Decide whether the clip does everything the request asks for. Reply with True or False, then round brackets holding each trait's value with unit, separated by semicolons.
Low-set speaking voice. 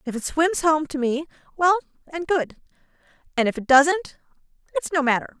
False (305 Hz)